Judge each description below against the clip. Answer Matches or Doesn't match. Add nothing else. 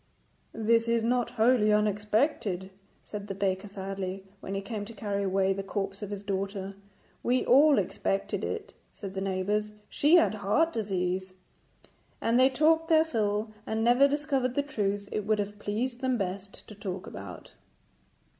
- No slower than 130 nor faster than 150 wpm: Doesn't match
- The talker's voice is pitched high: Matches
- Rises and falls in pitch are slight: Doesn't match